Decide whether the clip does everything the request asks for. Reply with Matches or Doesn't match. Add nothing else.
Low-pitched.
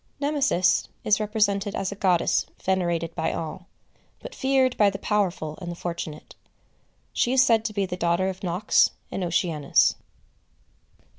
Doesn't match